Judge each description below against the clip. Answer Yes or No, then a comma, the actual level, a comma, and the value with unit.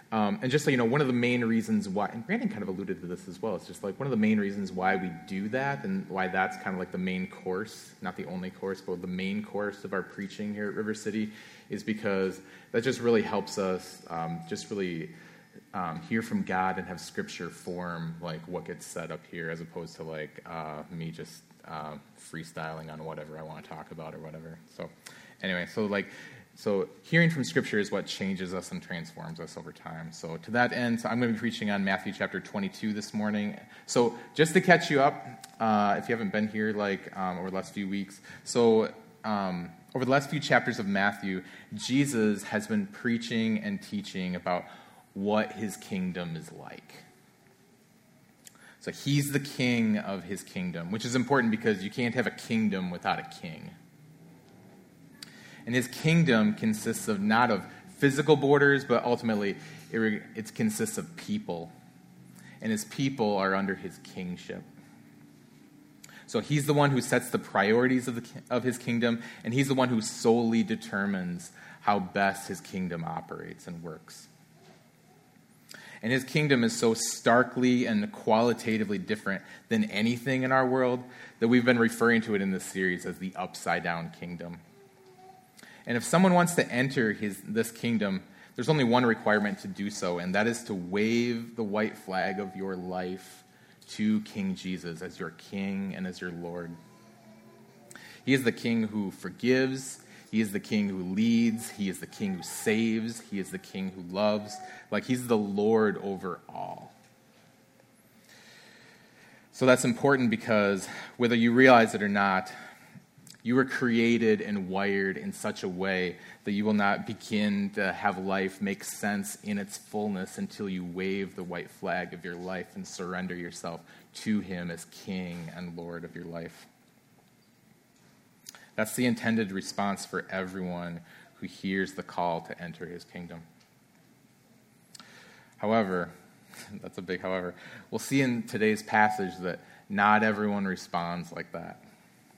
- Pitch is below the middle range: Yes, low, 110 Hz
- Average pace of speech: Yes, average, 175 wpm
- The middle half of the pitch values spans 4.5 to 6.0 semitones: Yes, wide, 5.6 semitones